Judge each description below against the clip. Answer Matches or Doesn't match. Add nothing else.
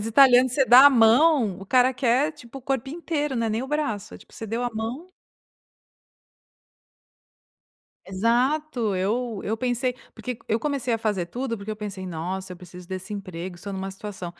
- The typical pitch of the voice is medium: Doesn't match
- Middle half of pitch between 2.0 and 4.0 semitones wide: Doesn't match